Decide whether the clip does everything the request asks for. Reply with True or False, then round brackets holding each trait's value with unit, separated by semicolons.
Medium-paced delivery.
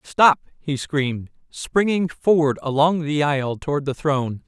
True (150 wpm)